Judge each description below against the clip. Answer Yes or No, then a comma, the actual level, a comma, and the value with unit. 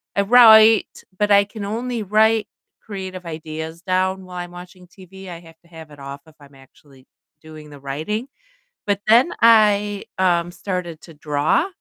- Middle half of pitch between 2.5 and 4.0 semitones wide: No, average, 4.6 semitones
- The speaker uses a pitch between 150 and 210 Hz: Yes, medium, 185 Hz